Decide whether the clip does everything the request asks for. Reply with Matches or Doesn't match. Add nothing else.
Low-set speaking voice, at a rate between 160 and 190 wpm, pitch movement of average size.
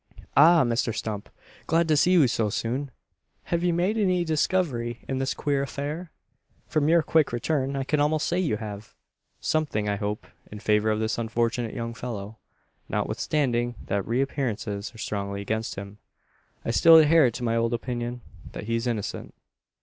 Doesn't match